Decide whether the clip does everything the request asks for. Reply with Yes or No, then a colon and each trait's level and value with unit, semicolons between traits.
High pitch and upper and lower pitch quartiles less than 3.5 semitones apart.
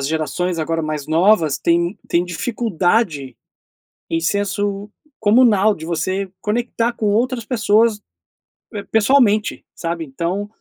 No: high, 200 Hz; average, 4.7 semitones